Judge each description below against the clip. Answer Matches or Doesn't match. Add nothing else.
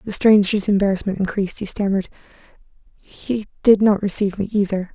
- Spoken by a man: Doesn't match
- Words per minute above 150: Doesn't match